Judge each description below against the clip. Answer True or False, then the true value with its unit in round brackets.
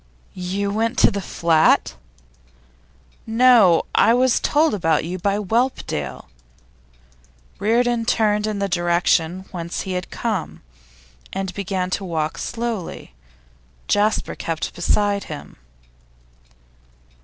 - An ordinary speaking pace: False (110 wpm)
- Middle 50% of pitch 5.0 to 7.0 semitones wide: False (4.3 semitones)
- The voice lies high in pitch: True (200 Hz)